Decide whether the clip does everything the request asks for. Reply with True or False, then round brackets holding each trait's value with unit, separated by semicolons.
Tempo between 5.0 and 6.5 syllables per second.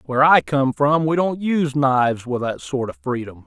True (5.2 syllables/s)